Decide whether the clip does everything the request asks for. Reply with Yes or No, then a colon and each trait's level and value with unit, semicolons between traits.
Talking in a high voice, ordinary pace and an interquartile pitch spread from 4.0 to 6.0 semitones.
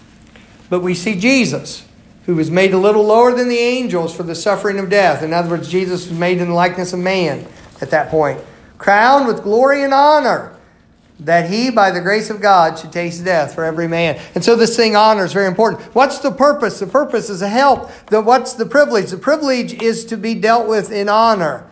No: high, 210 Hz; fast, 220 wpm; average, 4.6 semitones